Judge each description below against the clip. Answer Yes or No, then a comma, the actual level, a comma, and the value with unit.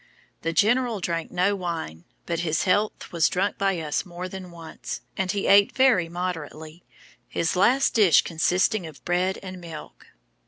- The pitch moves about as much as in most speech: Yes, average, 3.0 semitones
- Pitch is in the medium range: Yes, medium, 180 Hz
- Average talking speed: Yes, average, 160 wpm